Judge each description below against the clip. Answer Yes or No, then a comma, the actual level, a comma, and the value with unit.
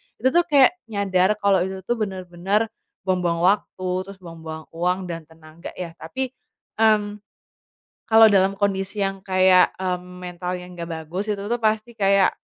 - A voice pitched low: No, high, 190 Hz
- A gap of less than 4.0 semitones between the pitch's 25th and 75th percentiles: Yes, average, 2.8 semitones